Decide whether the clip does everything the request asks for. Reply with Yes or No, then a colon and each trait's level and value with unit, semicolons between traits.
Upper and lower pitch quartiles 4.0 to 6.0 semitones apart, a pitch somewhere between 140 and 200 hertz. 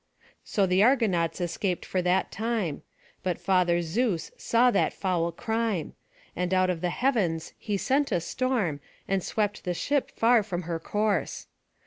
Yes: average, 4.4 semitones; high, 190 Hz